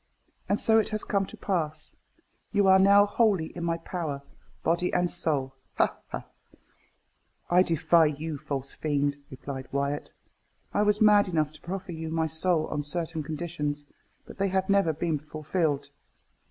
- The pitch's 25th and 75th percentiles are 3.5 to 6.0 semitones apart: Yes, average, 4.2 semitones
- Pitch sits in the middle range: Yes, medium, 165 Hz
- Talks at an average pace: Yes, average, 160 wpm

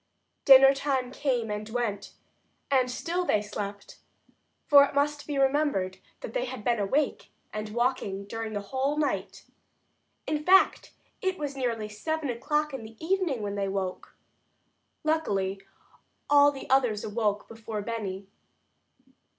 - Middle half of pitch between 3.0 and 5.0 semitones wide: No, wide, 5.6 semitones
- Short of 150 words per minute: Yes, average, 140 wpm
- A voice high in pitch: Yes, high, 245 Hz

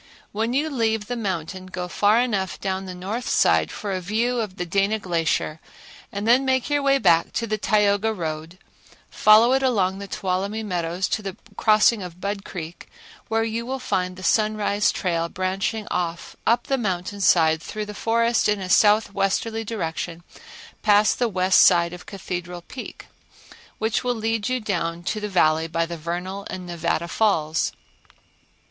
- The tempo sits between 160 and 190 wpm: Yes, average, 170 wpm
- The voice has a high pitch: Yes, high, 200 Hz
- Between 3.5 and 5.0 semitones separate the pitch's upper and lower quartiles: Yes, average, 3.9 semitones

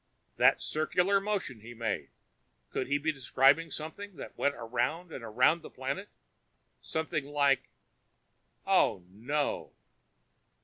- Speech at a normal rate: No, slow, 125 wpm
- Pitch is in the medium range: Yes, medium, 145 Hz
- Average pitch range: Yes, average, 4.4 semitones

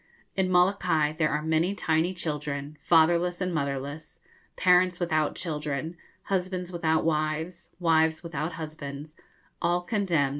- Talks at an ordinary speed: No, slow, 120 wpm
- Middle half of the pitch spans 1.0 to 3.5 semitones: Yes, narrow, 2.6 semitones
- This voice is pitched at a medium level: Yes, medium, 160 Hz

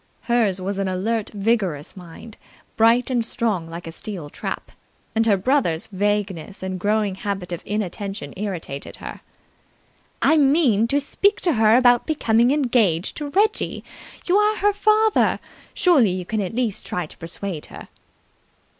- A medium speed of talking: Yes, average, 155 wpm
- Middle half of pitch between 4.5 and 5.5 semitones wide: Yes, average, 5.1 semitones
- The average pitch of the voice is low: No, high, 215 Hz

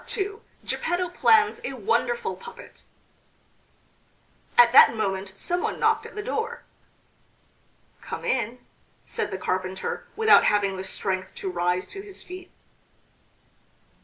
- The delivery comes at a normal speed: No, slow, 125 wpm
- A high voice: Yes, very high, 260 Hz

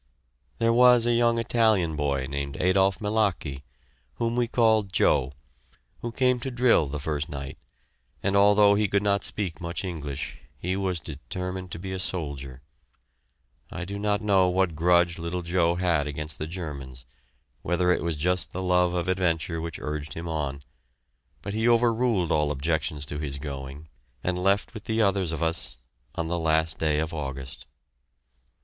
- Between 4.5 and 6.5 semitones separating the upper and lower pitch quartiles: Yes, average, 4.9 semitones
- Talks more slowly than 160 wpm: No, average, 170 wpm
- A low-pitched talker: Yes, very low, 85 Hz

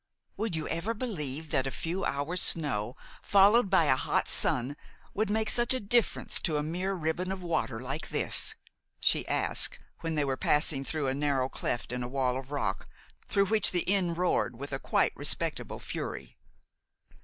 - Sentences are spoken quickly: No, average, 180 wpm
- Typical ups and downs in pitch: No, wide, 6.1 semitones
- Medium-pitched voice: Yes, medium, 160 Hz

